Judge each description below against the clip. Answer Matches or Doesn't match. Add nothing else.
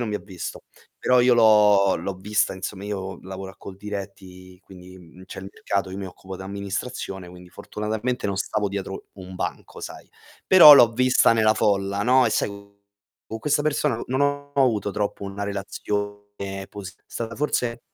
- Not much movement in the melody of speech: Doesn't match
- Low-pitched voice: Matches